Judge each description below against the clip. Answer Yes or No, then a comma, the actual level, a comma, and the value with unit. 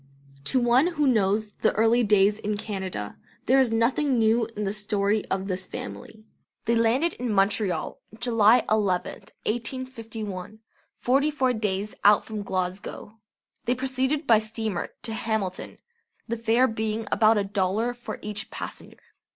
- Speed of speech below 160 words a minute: Yes, average, 145 wpm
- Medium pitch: No, high, 220 Hz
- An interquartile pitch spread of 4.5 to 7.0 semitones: No, average, 2.9 semitones